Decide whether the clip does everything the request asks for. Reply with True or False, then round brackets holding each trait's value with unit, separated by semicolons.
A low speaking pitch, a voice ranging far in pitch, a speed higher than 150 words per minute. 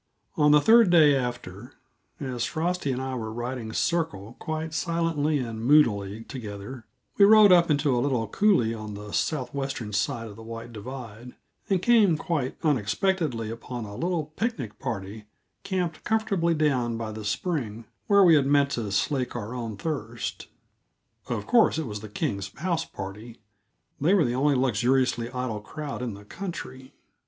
True (130 Hz; 5.9 semitones; 160 wpm)